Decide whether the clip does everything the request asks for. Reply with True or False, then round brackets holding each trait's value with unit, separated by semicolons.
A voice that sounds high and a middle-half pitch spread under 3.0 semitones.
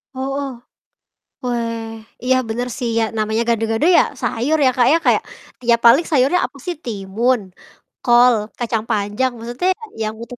True (240 Hz; 2.5 semitones)